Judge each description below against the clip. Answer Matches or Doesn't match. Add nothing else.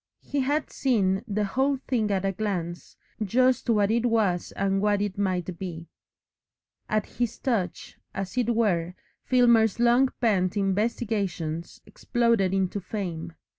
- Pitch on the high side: Matches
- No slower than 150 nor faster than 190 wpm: Doesn't match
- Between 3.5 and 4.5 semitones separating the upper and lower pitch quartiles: Matches